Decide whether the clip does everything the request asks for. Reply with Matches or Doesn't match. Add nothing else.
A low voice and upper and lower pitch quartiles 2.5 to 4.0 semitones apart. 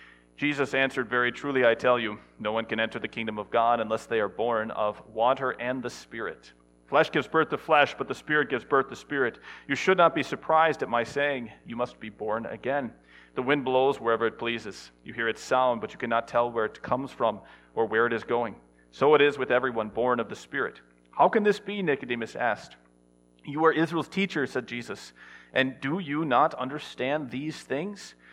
Doesn't match